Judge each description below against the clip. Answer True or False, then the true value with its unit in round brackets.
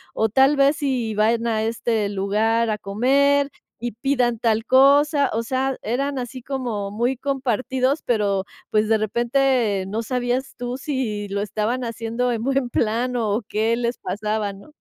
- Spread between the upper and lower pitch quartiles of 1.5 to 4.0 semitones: True (3.4 semitones)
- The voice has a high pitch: True (235 Hz)